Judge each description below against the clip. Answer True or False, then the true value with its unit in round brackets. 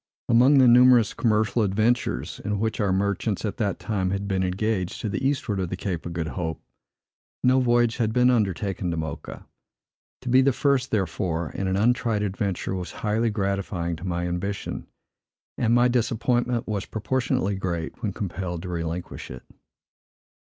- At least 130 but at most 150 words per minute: False (165 wpm)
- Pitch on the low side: True (100 Hz)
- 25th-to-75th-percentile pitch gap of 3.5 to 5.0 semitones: True (4.4 semitones)